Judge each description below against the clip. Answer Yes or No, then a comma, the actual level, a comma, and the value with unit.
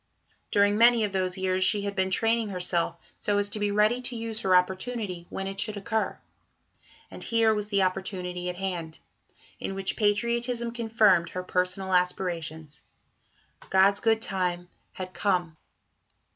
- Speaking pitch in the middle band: No, high, 195 Hz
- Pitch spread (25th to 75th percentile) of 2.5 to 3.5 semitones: Yes, average, 3.0 semitones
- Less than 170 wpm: Yes, average, 155 wpm